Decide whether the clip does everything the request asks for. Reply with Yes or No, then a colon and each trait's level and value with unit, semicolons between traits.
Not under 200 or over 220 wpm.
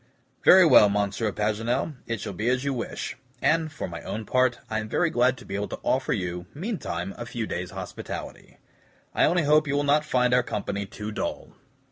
Yes: fast, 205 wpm